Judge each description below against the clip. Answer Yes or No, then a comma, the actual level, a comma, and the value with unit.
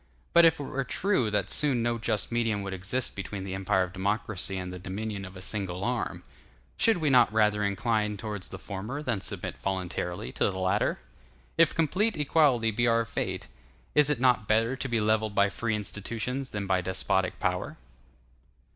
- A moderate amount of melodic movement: Yes, average, 4.3 semitones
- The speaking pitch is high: No, low, 105 Hz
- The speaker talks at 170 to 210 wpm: Yes, average, 190 wpm